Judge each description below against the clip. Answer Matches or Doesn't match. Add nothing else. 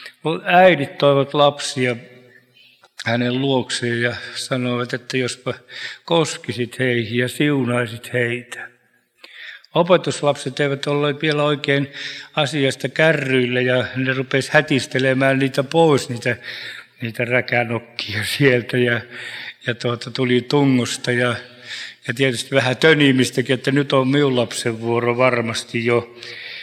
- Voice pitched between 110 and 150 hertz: Matches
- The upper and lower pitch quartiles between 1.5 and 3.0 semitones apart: Matches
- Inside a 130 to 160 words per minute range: Doesn't match